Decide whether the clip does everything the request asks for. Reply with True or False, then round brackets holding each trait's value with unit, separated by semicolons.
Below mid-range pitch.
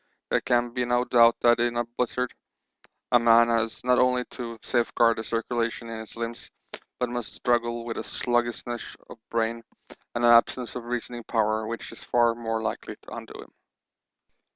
True (120 Hz)